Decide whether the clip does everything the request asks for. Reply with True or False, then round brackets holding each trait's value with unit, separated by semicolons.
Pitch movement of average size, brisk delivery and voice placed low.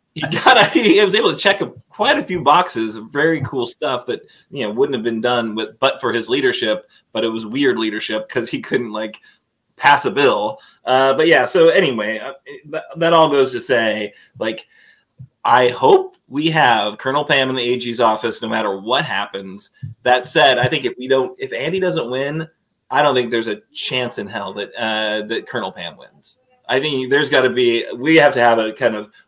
False (6.5 semitones; 215 wpm; 130 Hz)